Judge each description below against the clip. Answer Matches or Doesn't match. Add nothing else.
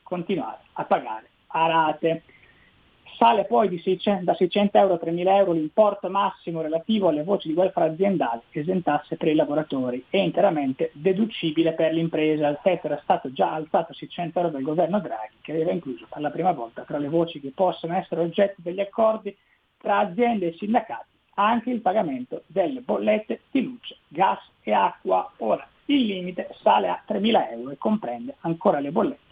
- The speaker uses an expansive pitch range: Doesn't match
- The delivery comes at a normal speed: Doesn't match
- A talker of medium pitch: Matches